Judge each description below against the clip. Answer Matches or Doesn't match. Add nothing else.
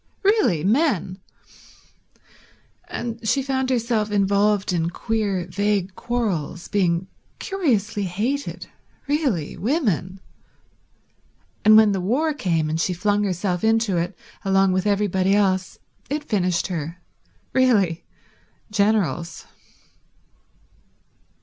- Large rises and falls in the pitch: Doesn't match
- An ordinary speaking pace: Doesn't match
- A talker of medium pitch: Doesn't match